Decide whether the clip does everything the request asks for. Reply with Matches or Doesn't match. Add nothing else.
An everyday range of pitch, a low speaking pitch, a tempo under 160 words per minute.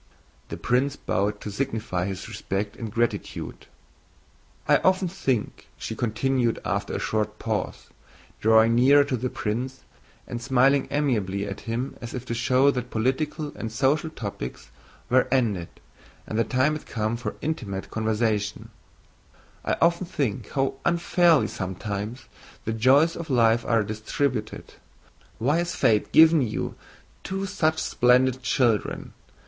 Matches